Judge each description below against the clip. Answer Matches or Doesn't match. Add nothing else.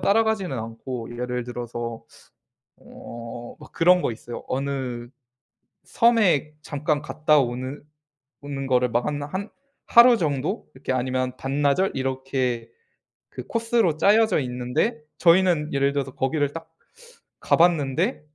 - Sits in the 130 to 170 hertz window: Matches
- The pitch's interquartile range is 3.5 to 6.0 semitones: Matches